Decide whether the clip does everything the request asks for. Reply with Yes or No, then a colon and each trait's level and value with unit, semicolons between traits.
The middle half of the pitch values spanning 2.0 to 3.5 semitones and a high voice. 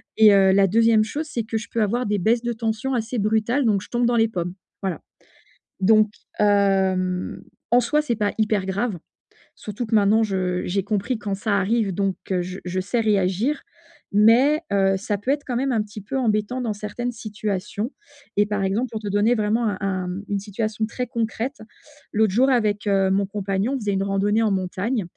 Yes: average, 2.9 semitones; high, 210 Hz